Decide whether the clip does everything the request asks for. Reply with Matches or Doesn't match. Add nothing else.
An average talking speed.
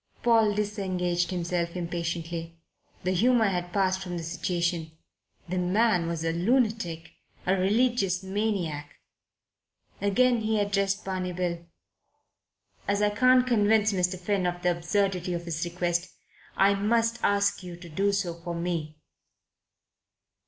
Doesn't match